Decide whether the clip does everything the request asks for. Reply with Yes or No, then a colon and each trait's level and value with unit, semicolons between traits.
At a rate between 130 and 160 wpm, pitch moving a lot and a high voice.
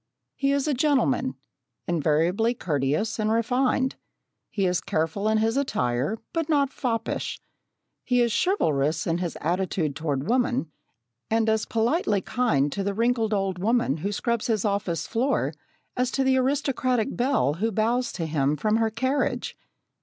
Yes: average, 155 wpm; wide, 6.7 semitones; high, 220 Hz